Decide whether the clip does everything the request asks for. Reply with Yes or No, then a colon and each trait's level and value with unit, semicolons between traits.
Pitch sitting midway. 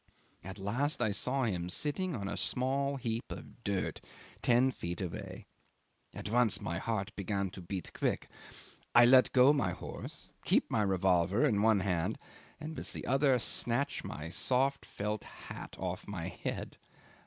No: low, 110 Hz